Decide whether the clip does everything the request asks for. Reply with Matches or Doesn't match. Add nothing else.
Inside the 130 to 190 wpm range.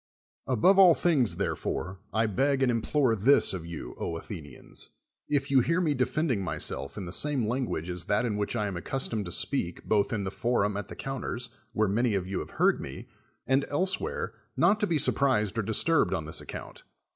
Doesn't match